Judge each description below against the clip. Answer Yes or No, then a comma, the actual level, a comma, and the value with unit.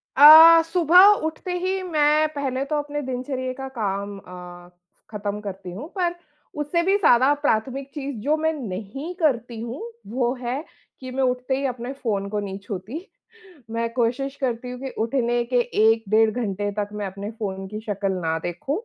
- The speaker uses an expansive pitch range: Yes, wide, 5.7 semitones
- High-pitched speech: Yes, very high, 250 Hz